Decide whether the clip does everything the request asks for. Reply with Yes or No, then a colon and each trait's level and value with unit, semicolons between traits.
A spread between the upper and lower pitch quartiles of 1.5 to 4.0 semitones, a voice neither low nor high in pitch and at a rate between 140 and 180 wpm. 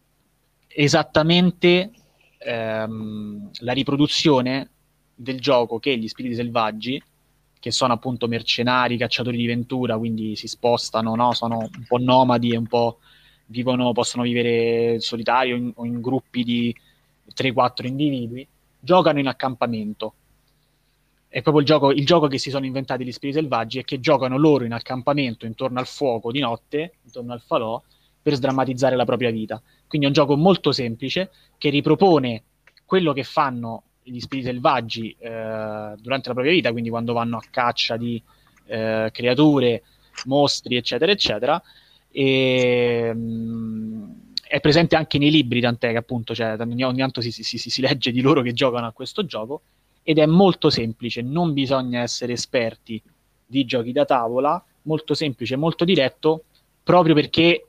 No: average, 3.5 semitones; low, 130 Hz; average, 150 wpm